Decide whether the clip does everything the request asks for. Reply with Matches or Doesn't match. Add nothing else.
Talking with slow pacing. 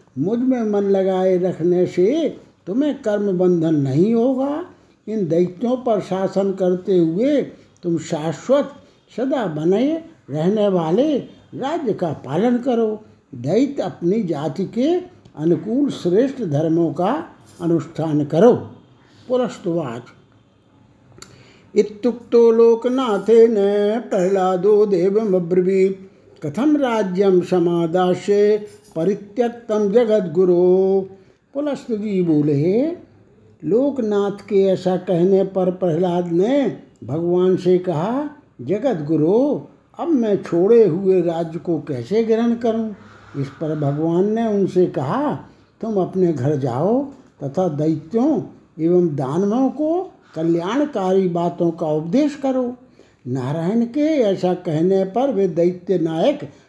Matches